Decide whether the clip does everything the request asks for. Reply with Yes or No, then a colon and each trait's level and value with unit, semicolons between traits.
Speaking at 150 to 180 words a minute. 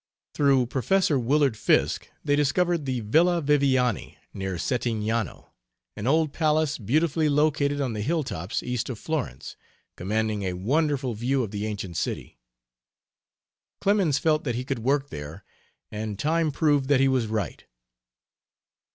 No: average, 140 wpm